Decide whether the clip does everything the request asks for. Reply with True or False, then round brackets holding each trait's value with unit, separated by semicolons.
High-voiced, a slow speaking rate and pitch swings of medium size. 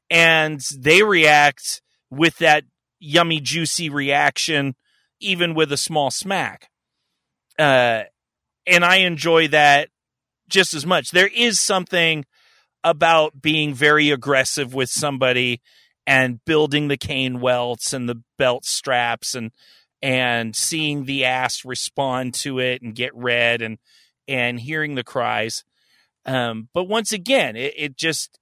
False (145 Hz; 130 wpm; 4.2 semitones)